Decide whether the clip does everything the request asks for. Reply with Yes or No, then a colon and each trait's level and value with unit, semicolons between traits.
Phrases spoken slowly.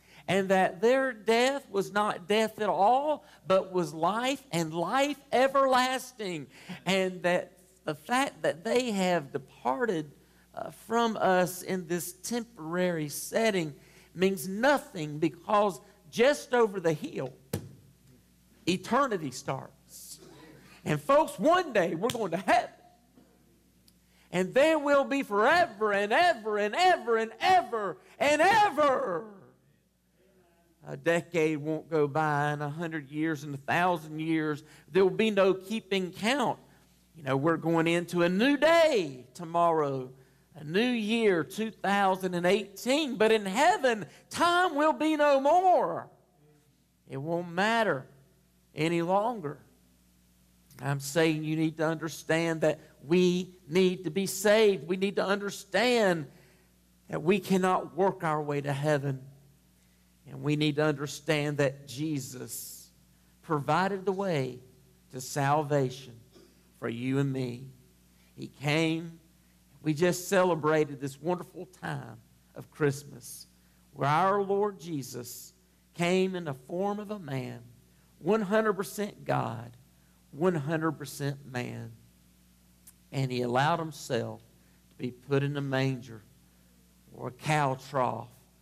Yes: slow, 125 wpm